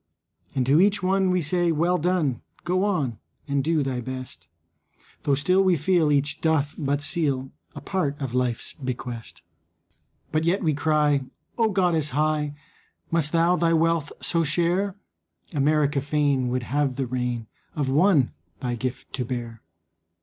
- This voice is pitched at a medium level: Yes, medium, 150 Hz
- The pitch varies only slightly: No, average, 4.3 semitones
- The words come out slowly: No, average, 155 wpm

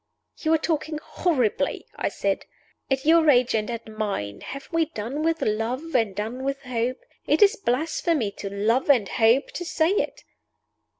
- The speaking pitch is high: Yes, very high, 260 Hz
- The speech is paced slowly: No, average, 170 wpm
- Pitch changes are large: Yes, wide, 6.0 semitones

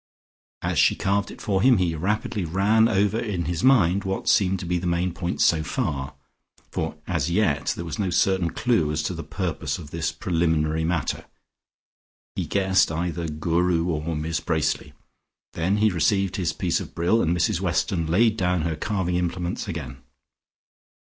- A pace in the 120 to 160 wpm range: No, average, 175 wpm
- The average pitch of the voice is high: No, very low, 90 Hz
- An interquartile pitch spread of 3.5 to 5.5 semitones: No, average, 3.0 semitones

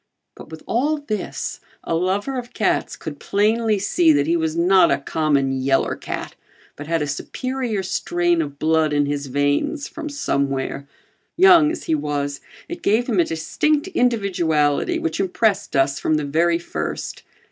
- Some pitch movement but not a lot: No, wide, 7.8 semitones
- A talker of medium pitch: Yes, medium, 170 Hz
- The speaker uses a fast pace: No, average, 165 wpm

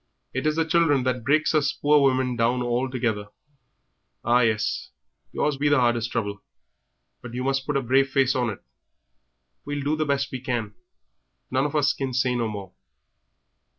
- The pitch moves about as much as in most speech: Yes, average, 3.0 semitones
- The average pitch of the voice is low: Yes, low, 130 Hz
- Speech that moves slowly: No, average, 175 wpm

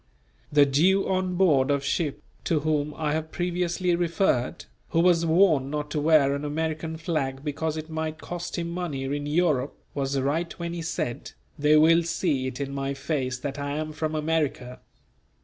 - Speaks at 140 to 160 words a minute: No, average, 180 wpm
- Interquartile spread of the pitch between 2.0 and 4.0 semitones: Yes, average, 2.9 semitones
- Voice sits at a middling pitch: Yes, medium, 155 Hz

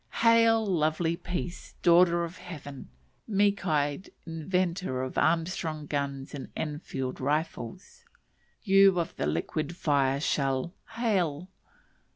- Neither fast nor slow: No, slow, 110 wpm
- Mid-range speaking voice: Yes, medium, 165 Hz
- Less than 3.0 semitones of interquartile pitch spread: No, average, 4.3 semitones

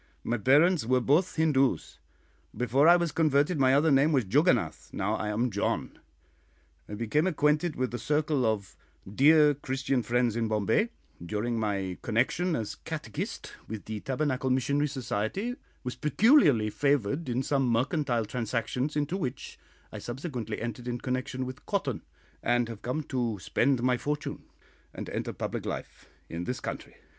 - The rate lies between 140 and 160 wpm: Yes, average, 155 wpm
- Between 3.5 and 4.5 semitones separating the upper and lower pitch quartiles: Yes, average, 4.2 semitones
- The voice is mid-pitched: No, low, 130 Hz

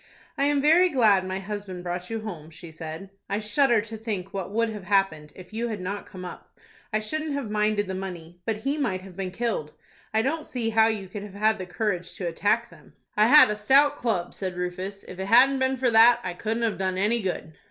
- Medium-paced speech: No, fast, 235 wpm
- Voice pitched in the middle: No, high, 210 Hz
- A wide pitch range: No, average, 3.8 semitones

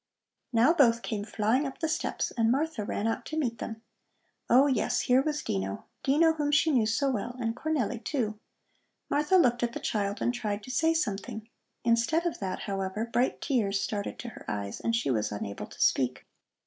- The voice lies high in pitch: Yes, high, 235 Hz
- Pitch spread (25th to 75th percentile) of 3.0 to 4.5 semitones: No, average, 5.2 semitones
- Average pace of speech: Yes, average, 195 wpm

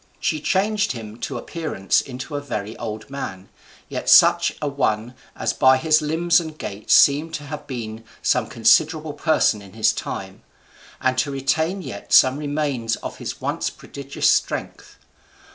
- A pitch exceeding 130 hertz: Yes, medium, 140 Hz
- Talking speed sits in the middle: Yes, average, 160 wpm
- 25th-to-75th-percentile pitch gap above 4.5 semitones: Yes, wide, 5.4 semitones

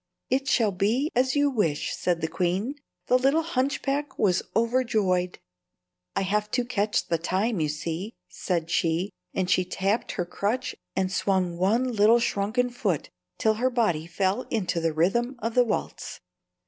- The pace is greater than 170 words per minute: No, average, 160 wpm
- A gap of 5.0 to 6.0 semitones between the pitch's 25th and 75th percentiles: Yes, wide, 5.4 semitones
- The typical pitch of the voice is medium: No, high, 210 Hz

